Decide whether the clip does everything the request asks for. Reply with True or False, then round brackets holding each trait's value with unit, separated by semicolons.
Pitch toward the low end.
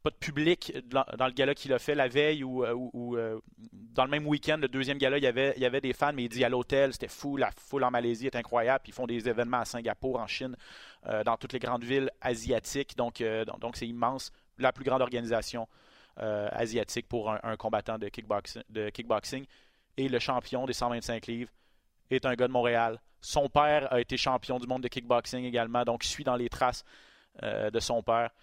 True (125 Hz)